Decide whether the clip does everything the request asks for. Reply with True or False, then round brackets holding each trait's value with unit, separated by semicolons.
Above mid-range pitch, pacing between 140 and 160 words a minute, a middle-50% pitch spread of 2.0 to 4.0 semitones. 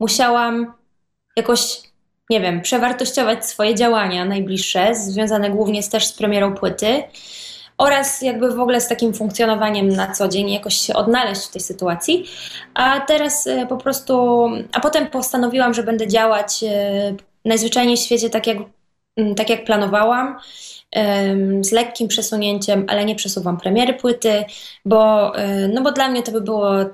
True (220 Hz; 145 wpm; 3.0 semitones)